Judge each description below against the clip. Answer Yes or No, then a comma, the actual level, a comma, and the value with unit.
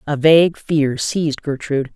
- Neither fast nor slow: Yes, average, 155 wpm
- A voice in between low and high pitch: Yes, medium, 145 Hz